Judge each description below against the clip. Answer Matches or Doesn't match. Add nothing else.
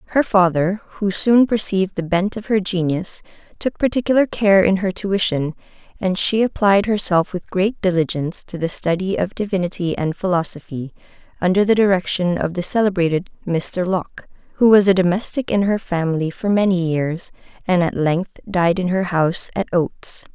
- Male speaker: Doesn't match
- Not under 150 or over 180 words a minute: Matches